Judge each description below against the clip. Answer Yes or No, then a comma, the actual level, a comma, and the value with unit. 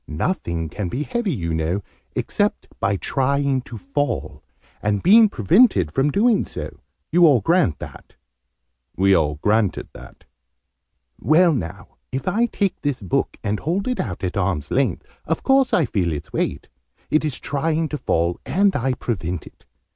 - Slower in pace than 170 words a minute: Yes, average, 160 wpm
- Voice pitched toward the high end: No, low, 130 Hz